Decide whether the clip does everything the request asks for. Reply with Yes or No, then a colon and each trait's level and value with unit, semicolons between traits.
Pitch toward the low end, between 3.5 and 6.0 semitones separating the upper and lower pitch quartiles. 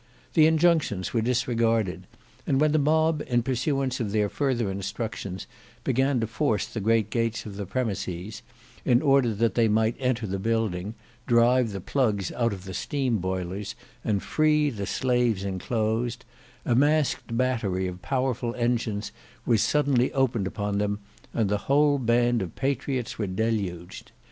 Yes: low, 115 Hz; average, 4.1 semitones